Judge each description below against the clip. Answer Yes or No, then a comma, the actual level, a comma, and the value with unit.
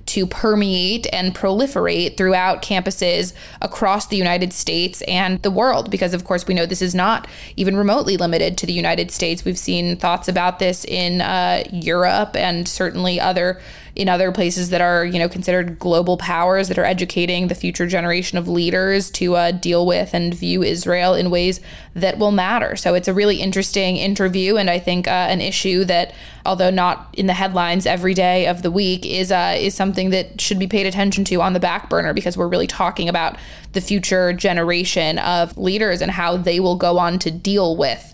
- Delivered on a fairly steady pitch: Yes, narrow, 1.4 semitones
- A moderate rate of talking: Yes, average, 195 wpm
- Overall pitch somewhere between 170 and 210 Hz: Yes, medium, 185 Hz